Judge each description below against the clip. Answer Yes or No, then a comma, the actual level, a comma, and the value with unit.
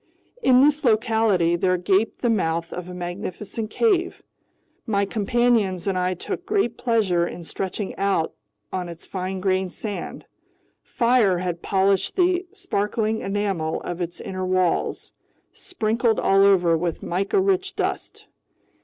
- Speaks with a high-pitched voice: Yes, high, 195 Hz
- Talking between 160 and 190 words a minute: No, slow, 135 wpm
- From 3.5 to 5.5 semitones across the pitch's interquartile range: Yes, average, 4.2 semitones